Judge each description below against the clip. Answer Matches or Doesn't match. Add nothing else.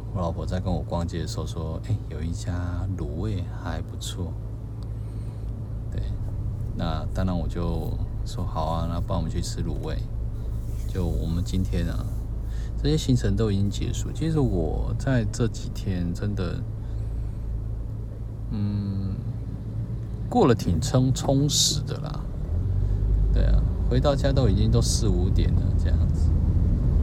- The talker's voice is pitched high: Doesn't match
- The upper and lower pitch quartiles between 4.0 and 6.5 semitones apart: Doesn't match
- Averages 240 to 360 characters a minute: Doesn't match